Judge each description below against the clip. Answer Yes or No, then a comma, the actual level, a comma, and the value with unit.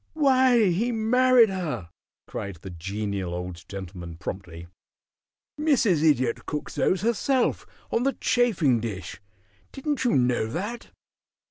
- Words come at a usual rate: No, slow, 120 wpm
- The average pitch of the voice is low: No, medium, 155 Hz